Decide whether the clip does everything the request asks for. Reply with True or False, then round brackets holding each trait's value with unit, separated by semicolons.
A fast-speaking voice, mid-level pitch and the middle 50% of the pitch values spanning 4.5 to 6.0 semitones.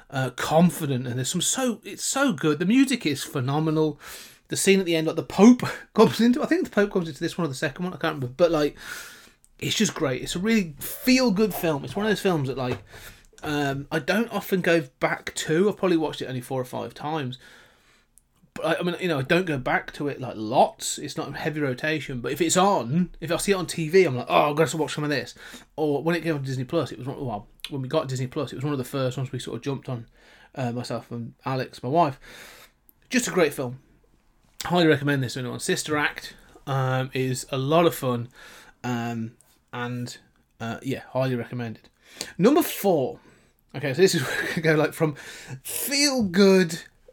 True (225 wpm; 155 Hz; 5.3 semitones)